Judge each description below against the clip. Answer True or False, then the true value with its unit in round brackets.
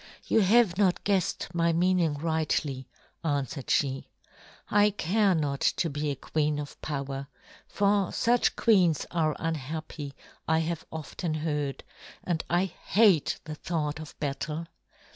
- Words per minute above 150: False (135 wpm)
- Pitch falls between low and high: True (160 Hz)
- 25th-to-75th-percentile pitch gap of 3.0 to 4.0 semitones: True (3.6 semitones)